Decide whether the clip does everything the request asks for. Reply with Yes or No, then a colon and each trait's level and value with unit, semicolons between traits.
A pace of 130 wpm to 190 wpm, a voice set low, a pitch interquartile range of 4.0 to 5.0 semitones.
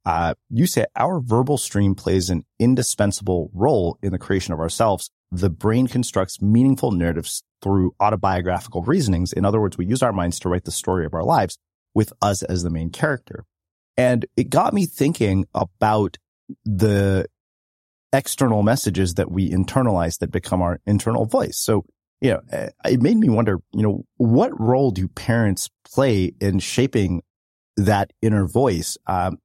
Yes: average, 165 wpm; low, 100 Hz; average, 4.4 semitones